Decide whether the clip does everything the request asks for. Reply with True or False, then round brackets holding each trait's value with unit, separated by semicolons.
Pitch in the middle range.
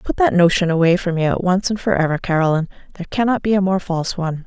True (180 Hz)